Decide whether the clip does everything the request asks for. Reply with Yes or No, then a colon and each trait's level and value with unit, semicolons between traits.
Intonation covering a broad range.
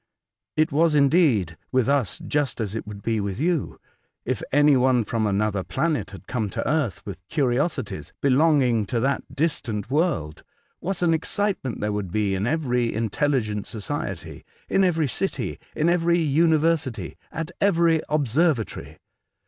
Yes: wide, 6.9 semitones